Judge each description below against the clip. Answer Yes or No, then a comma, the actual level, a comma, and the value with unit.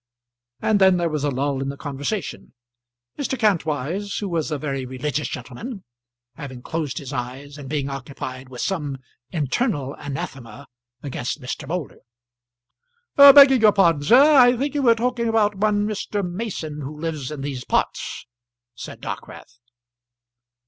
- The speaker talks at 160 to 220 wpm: No, average, 150 wpm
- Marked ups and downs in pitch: Yes, wide, 7.2 semitones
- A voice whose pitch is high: No, medium, 150 Hz